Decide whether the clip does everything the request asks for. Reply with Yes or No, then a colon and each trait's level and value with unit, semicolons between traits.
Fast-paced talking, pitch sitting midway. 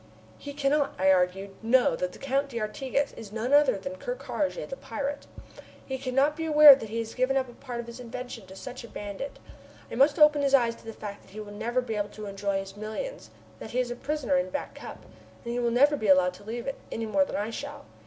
No: fast, 245 wpm; high, 240 Hz